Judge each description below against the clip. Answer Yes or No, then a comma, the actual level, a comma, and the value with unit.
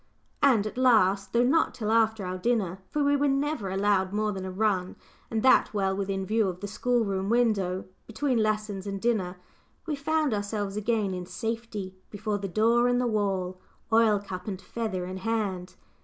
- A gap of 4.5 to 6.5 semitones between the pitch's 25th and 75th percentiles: No, average, 3.3 semitones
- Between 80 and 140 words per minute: No, average, 185 wpm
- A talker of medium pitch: No, high, 210 Hz